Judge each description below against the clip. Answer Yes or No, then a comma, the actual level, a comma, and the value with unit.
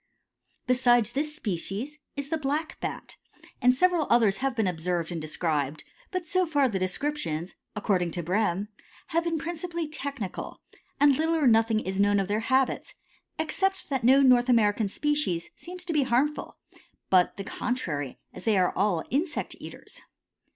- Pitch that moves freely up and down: Yes, wide, 7.6 semitones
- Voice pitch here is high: Yes, high, 245 Hz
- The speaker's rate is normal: Yes, average, 160 wpm